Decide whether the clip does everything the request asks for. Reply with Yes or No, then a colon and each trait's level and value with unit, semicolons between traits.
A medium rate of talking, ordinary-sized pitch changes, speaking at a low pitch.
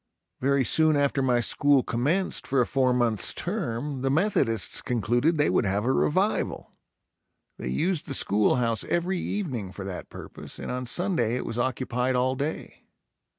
Yes: average, 165 wpm; average, 4.0 semitones; low, 130 Hz